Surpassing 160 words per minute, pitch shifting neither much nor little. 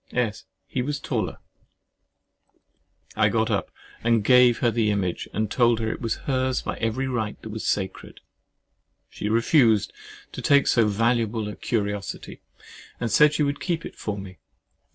Yes: average, 170 wpm; average, 3.0 semitones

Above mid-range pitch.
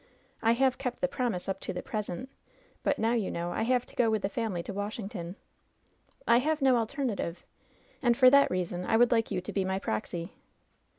Yes: high, 220 Hz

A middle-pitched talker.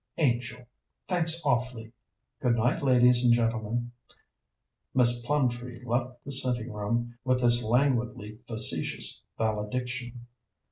No: low, 120 Hz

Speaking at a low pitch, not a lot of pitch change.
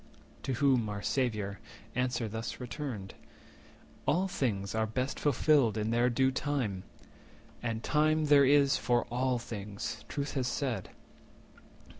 No: low, 125 Hz; average, 4.1 semitones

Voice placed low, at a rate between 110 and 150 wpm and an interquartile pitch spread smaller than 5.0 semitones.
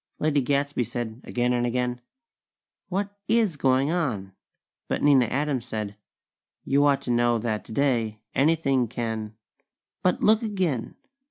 Yes: low, 130 Hz; average, 140 wpm; average, 3.9 semitones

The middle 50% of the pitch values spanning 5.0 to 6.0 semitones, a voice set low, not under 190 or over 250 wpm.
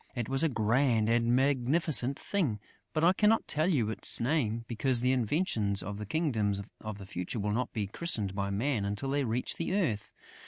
Yes: wide, 5.4 semitones; low, 120 Hz; average, 195 wpm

